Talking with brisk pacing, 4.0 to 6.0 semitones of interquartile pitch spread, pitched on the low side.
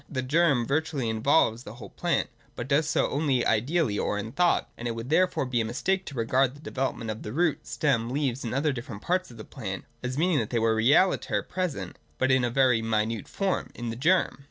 Yes: fast, 230 wpm; average, 4.7 semitones; low, 130 Hz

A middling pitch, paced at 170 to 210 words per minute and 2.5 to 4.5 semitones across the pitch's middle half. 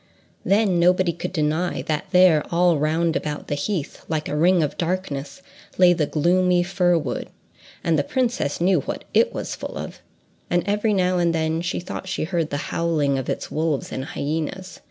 Yes: medium, 170 Hz; average, 185 wpm; average, 3.0 semitones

